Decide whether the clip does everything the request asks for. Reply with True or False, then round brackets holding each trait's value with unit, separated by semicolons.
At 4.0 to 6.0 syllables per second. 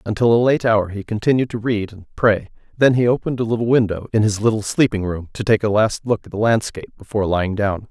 False (6.4 syllables/s)